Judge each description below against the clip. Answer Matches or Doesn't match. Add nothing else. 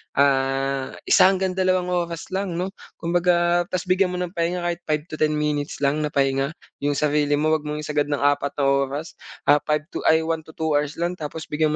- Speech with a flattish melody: Doesn't match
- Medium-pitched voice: Matches